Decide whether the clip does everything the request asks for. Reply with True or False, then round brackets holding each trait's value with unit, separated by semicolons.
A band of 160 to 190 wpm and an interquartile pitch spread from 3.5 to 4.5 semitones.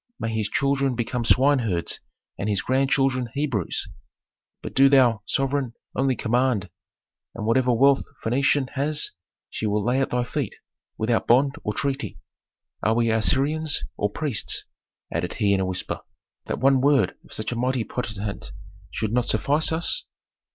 False (150 wpm; 3.8 semitones)